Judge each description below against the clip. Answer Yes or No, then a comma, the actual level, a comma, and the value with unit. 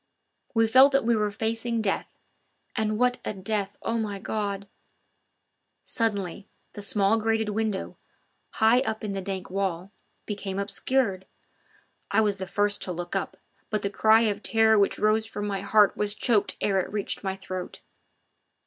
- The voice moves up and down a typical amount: No, narrow, 2.1 semitones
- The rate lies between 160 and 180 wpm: Yes, average, 165 wpm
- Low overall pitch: No, high, 210 Hz